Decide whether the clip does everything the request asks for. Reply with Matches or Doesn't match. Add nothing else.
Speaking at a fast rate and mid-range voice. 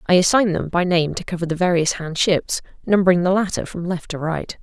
Matches